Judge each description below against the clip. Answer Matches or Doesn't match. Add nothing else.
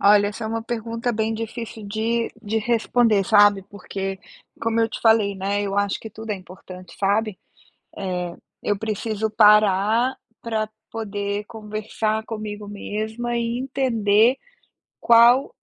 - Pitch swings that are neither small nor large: Doesn't match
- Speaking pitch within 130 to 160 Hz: Doesn't match